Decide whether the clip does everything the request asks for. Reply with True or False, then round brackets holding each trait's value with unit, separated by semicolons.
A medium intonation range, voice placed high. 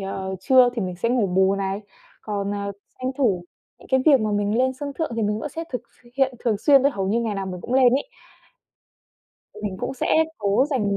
True (4.7 semitones; 215 Hz)